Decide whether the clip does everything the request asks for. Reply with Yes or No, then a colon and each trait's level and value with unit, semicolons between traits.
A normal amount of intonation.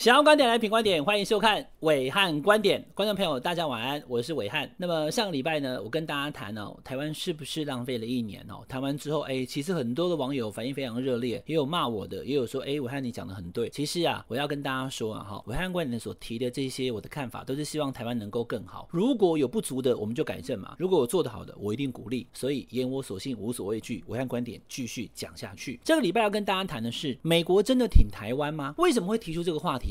No: wide, 5.7 semitones